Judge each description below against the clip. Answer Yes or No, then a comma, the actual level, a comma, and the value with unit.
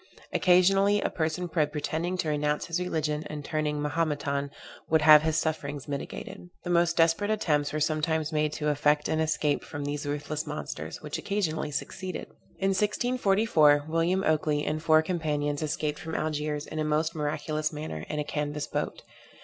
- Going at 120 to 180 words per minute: Yes, average, 165 wpm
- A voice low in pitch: No, medium, 155 Hz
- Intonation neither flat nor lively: No, narrow, 1.9 semitones